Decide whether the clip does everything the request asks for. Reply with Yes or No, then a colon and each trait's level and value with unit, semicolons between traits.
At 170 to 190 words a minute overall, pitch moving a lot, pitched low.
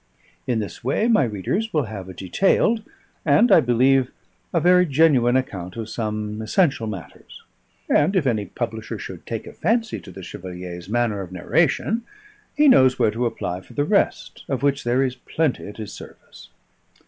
Yes: average, 175 wpm; wide, 6.7 semitones; low, 120 Hz